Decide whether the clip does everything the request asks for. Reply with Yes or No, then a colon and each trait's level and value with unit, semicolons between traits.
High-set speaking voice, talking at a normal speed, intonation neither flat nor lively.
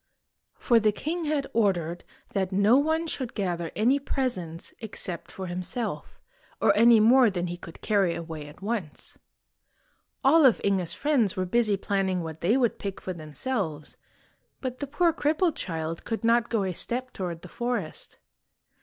No: high, 205 Hz; average, 165 wpm; wide, 6.2 semitones